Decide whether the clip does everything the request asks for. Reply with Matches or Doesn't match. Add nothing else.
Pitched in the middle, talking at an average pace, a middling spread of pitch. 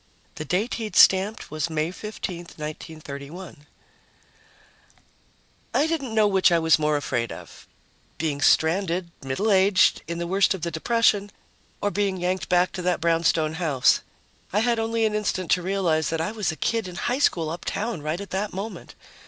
Matches